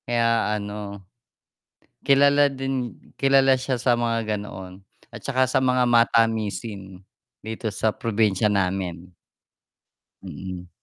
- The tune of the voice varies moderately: Yes, average, 4.1 semitones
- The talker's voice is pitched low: Yes, low, 115 Hz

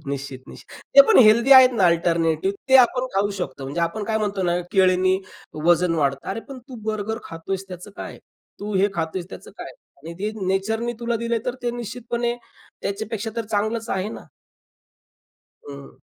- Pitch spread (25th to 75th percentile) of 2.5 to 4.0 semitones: No, average, 4.8 semitones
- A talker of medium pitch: No, high, 200 Hz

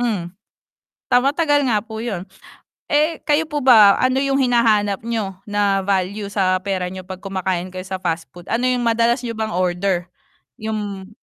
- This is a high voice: Yes, high, 210 Hz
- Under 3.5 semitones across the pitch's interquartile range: No, average, 4.4 semitones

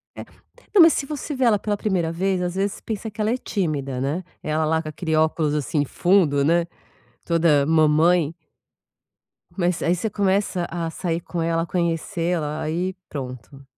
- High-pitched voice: No, medium, 170 Hz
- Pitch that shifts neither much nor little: Yes, average, 3.7 semitones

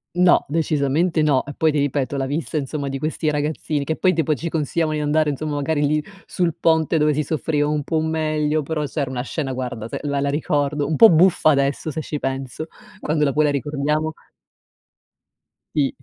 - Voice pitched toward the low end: No, medium, 150 Hz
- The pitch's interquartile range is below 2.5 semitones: Yes, narrow, 1.9 semitones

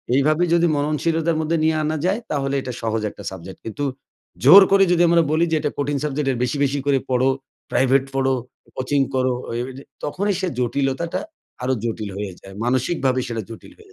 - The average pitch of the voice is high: No, medium, 140 Hz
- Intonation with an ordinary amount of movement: Yes, average, 3.9 semitones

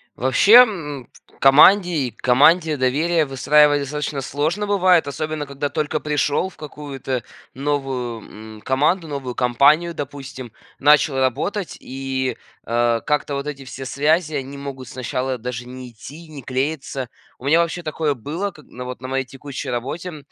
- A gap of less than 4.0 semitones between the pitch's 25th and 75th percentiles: Yes, average, 3.0 semitones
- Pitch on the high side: No, medium, 140 Hz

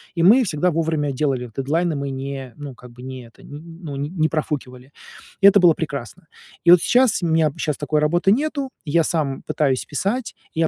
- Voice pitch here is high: No, medium, 155 Hz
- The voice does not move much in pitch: No, average, 3.9 semitones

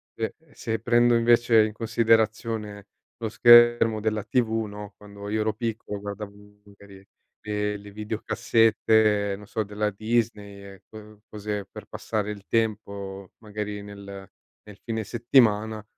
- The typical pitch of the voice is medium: No, low, 105 Hz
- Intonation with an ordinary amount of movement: No, narrow, 1.7 semitones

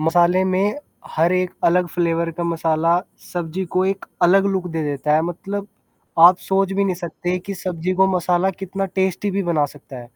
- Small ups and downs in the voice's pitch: Yes, narrow, 2.3 semitones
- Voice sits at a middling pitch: Yes, medium, 180 Hz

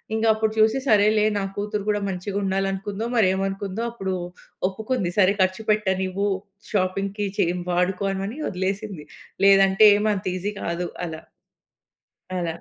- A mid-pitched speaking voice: No, high, 195 Hz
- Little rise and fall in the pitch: Yes, narrow, 2.0 semitones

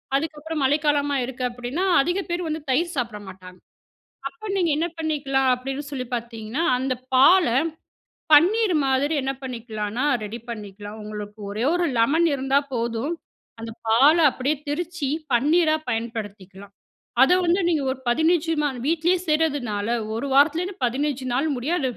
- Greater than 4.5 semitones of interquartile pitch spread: Yes, wide, 5.4 semitones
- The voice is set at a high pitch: Yes, very high, 270 Hz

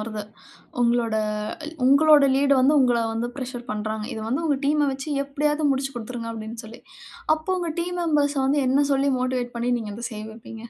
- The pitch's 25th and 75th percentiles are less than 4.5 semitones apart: Yes, average, 3.9 semitones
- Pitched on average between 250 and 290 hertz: Yes, very high, 255 Hz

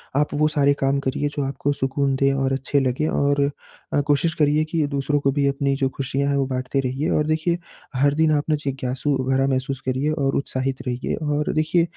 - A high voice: No, medium, 140 Hz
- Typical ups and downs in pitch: No, narrow, 1.7 semitones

